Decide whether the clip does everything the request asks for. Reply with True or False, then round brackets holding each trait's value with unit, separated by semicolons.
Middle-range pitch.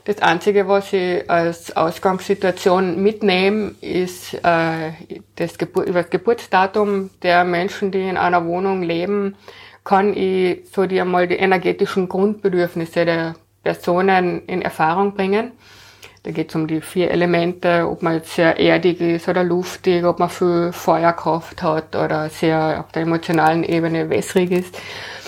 True (180 Hz)